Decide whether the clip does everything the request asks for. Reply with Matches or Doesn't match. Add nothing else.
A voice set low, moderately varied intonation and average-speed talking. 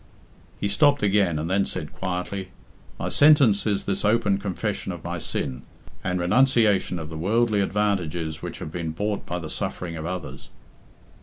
Matches